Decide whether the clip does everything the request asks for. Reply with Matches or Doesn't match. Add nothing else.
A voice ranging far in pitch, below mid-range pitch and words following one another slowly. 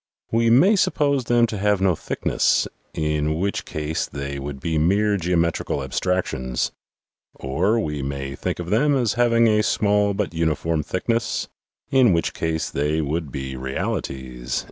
Doesn't match